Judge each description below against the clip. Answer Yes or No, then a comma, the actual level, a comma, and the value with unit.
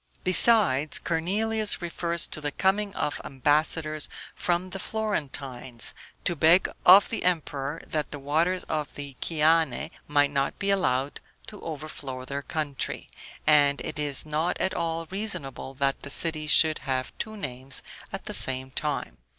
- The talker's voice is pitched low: No, medium, 155 Hz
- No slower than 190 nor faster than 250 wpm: No, average, 150 wpm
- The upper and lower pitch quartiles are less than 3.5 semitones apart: No, average, 4.1 semitones